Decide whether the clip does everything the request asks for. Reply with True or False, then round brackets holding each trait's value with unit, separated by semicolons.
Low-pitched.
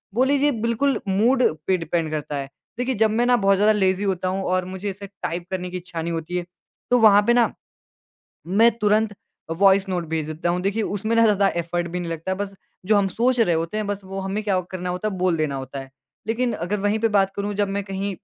False (195 Hz)